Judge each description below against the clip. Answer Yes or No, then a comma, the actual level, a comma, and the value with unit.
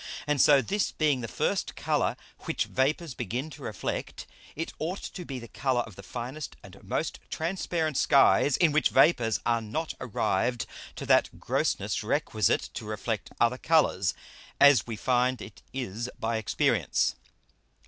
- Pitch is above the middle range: No, low, 130 Hz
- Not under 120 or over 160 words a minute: Yes, average, 155 wpm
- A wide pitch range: No, average, 4.9 semitones